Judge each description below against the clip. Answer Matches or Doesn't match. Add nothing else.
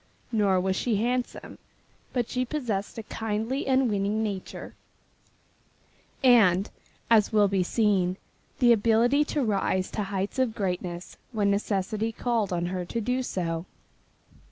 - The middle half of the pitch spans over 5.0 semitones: Doesn't match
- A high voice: Matches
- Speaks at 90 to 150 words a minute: Matches